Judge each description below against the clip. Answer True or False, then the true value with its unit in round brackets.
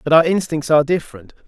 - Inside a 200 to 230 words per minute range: True (205 wpm)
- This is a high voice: False (155 Hz)